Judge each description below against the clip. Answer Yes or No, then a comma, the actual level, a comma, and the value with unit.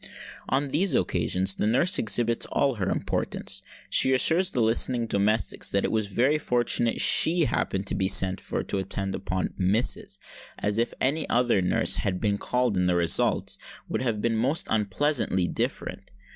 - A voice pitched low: Yes, low, 110 Hz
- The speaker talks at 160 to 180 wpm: Yes, average, 170 wpm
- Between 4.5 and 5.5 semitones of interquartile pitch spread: Yes, average, 4.8 semitones